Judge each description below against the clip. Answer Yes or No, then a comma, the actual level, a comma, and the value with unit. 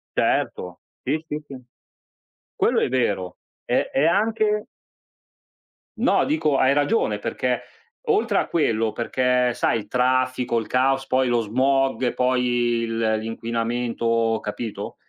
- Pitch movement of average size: Yes, average, 3.1 semitones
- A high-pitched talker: No, low, 125 Hz